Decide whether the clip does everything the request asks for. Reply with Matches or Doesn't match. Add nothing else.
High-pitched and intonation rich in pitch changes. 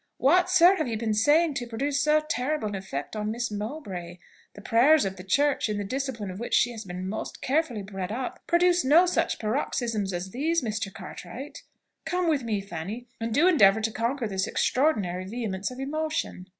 Matches